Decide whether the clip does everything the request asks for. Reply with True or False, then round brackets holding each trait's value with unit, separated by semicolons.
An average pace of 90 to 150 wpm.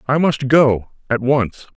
True (135 wpm)